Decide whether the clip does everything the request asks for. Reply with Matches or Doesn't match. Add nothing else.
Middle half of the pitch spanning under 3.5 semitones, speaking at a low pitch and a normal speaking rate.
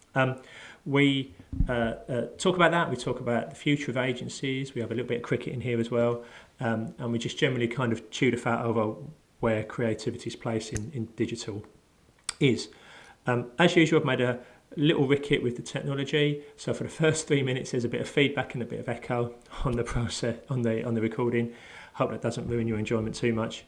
Doesn't match